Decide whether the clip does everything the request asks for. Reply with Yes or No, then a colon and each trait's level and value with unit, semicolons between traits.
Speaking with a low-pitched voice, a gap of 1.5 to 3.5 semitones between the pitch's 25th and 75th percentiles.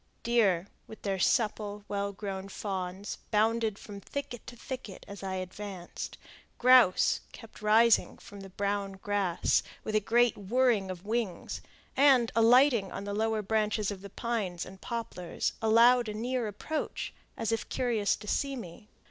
No: high, 210 Hz; average, 3.0 semitones